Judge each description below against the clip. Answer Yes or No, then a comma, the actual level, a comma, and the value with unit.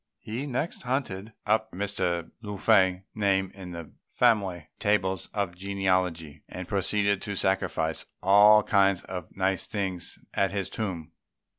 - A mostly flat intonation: Yes, narrow, 2.2 semitones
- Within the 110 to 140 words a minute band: Yes, slow, 135 wpm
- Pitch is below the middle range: Yes, very low, 95 Hz